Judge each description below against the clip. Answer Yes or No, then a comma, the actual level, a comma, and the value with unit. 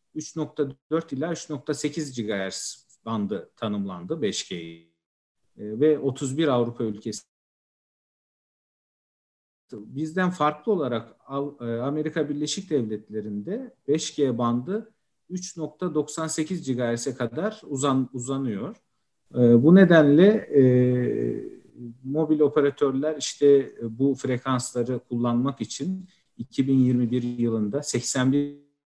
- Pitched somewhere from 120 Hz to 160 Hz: Yes, medium, 140 Hz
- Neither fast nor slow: No, slow, 80 wpm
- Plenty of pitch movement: No, average, 4.2 semitones